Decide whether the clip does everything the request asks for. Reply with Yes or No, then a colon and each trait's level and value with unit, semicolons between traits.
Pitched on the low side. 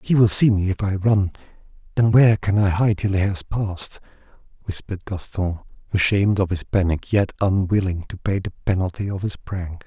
Yes: very low, 95 Hz